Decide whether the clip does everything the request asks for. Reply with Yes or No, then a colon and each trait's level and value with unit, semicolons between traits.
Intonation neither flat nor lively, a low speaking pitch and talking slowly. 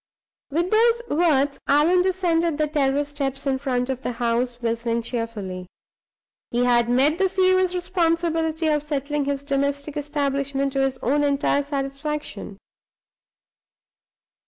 No: average, 3.4 semitones; very high, 285 Hz; slow, 130 wpm